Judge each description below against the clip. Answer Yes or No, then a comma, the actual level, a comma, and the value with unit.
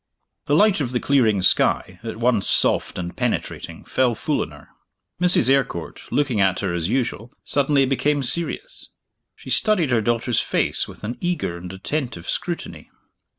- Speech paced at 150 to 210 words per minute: Yes, average, 160 wpm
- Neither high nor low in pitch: No, low, 125 Hz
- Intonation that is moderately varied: No, wide, 6.0 semitones